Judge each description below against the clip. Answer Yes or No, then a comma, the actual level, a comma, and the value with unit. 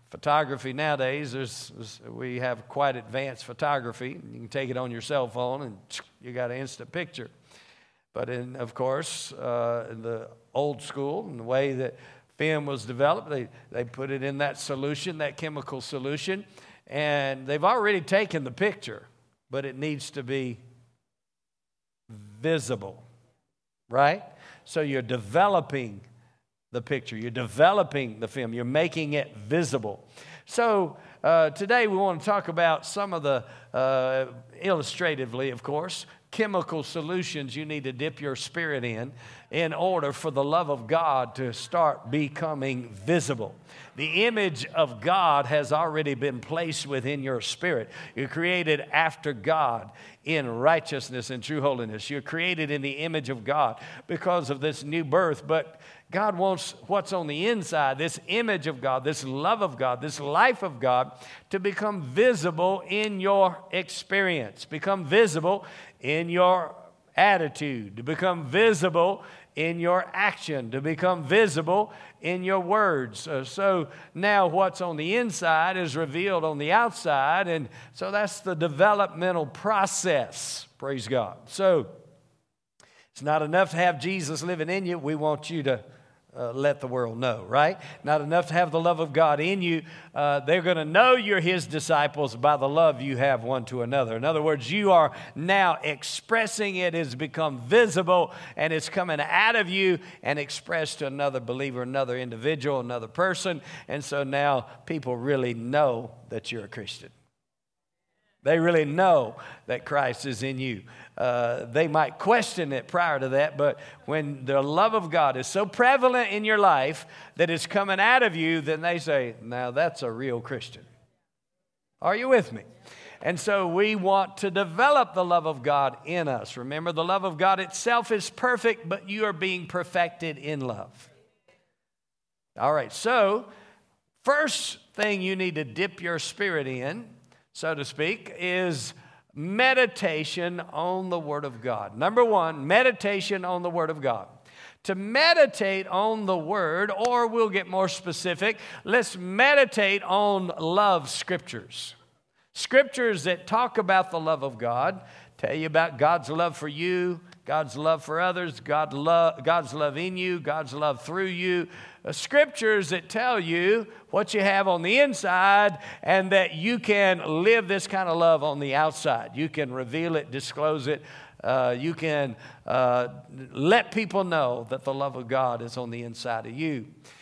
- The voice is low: No, medium, 155 Hz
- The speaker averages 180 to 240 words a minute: No, average, 160 wpm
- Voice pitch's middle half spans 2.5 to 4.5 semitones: No, wide, 5.6 semitones